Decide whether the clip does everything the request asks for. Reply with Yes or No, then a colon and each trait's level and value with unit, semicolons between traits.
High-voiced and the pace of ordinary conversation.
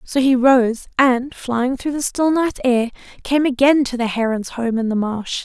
No: very high, 255 Hz; fast, 210 wpm